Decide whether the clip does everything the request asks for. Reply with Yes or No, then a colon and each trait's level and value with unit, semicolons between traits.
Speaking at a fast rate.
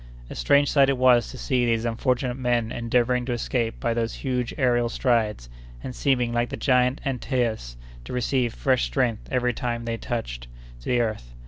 No: average, 180 wpm